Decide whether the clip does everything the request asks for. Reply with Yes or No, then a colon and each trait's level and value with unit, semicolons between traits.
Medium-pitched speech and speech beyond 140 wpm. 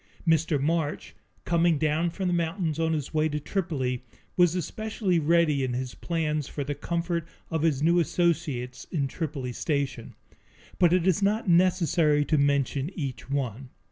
Yes: medium, 160 Hz; average, 160 wpm